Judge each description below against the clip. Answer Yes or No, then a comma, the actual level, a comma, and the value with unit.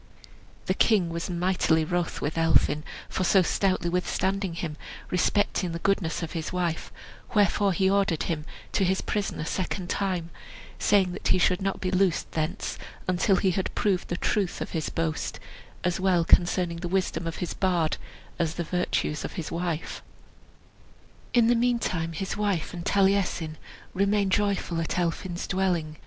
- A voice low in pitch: No, medium, 180 Hz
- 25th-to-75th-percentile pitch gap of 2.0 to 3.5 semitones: Yes, narrow, 2.5 semitones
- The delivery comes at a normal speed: Yes, average, 165 wpm